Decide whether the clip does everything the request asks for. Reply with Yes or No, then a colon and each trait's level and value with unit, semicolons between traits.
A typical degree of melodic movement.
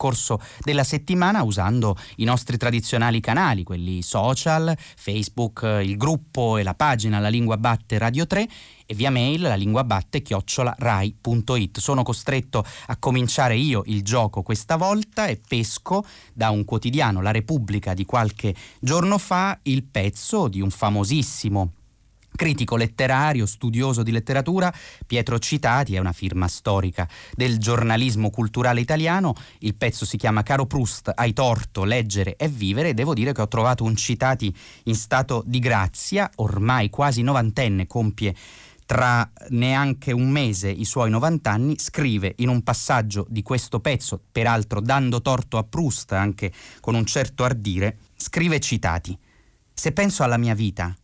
Yes: average, 4.1 semitones